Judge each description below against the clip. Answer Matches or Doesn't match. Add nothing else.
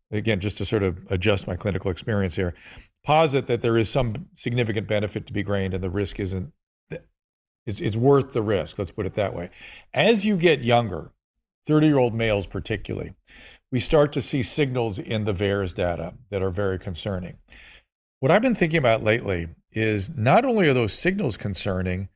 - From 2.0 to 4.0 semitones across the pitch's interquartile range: Doesn't match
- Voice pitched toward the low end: Matches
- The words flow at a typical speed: Matches